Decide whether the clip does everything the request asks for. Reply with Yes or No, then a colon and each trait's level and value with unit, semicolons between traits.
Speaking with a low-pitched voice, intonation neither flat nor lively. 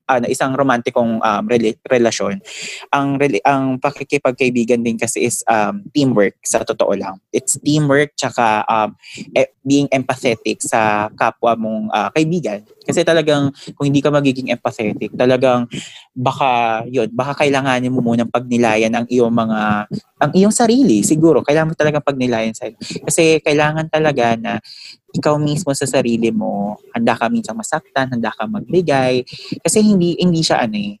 Yes: low, 130 Hz; average, 4.4 semitones